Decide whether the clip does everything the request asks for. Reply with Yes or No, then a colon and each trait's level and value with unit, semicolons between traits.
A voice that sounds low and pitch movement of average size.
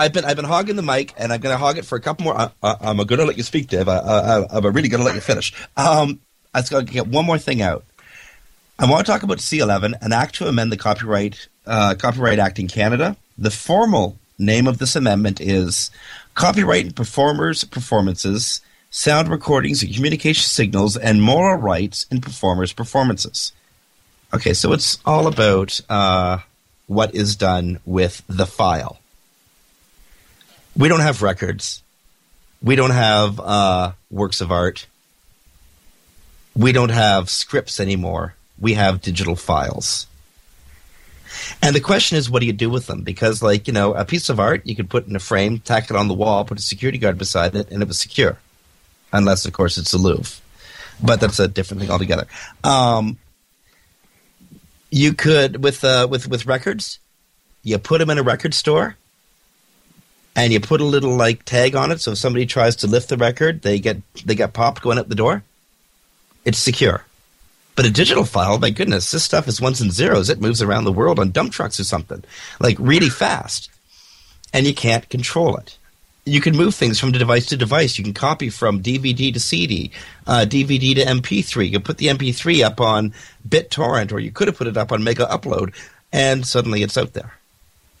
Yes: low, 115 Hz; average, 5.0 semitones